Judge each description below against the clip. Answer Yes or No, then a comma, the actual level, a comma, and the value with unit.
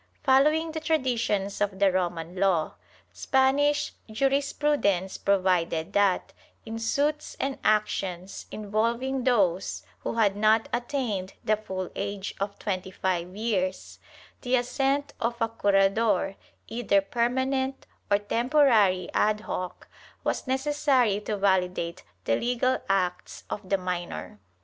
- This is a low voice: No, high, 210 Hz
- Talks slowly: Yes, slow, 120 wpm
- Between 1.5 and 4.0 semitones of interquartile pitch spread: No, wide, 5.4 semitones